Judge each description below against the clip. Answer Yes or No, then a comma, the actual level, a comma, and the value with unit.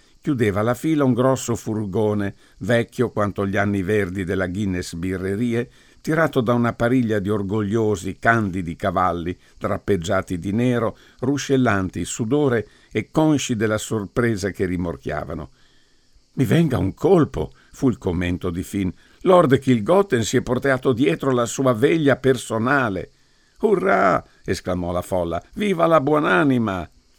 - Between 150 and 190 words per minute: No, average, 130 wpm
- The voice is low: Yes, low, 110 Hz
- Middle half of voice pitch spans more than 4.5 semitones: Yes, average, 5.2 semitones